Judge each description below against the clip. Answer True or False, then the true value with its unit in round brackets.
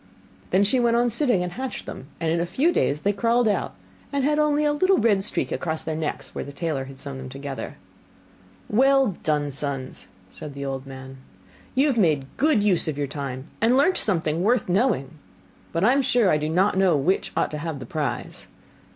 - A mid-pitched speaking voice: True (175 Hz)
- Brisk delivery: True (215 wpm)